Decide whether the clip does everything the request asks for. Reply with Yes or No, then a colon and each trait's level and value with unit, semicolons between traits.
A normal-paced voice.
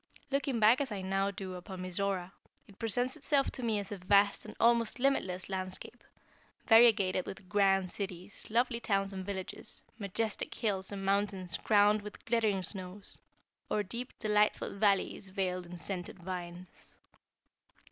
Yes: average, 145 wpm